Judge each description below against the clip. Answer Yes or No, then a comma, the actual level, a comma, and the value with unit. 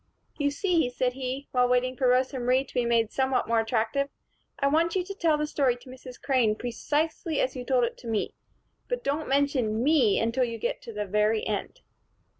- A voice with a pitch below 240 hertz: No, very high, 255 Hz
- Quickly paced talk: Yes, fast, 210 wpm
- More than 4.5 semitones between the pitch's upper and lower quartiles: No, average, 3.4 semitones